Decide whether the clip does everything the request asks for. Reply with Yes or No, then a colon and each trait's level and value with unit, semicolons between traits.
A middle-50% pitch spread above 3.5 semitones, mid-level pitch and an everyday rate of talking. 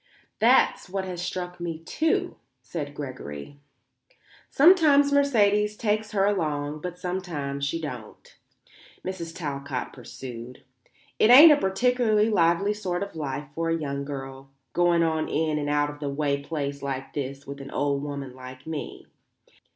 Yes: wide, 5.6 semitones; medium, 160 Hz; average, 150 wpm